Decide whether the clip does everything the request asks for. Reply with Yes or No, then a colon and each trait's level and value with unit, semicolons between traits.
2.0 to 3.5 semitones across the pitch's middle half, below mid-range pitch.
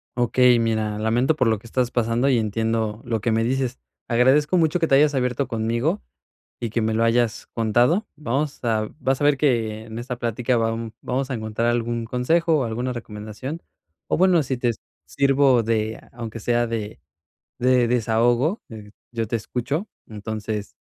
Yes: average, 2.8 semitones; low, 120 Hz